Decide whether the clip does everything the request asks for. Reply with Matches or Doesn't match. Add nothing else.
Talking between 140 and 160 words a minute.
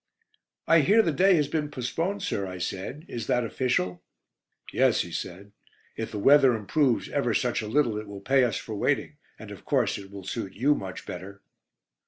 Doesn't match